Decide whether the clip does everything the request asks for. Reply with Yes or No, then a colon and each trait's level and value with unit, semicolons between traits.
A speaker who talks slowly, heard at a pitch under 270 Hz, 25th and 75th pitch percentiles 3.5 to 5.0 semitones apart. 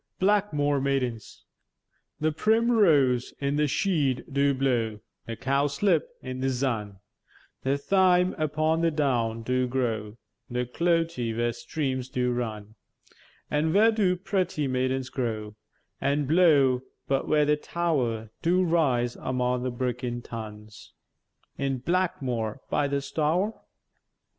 Yes: slow, 125 wpm; low, 135 Hz; average, 4.6 semitones